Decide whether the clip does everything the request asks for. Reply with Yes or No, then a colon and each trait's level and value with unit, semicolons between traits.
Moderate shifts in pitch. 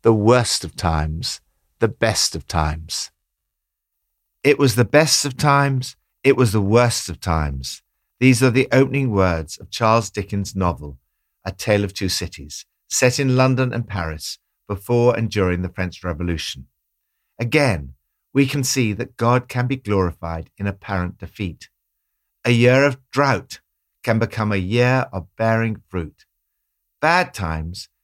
No: wide, 6.2 semitones